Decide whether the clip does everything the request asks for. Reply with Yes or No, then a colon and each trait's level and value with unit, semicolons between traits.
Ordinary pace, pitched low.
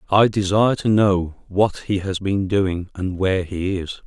Yes: average, 190 wpm; very low, 95 Hz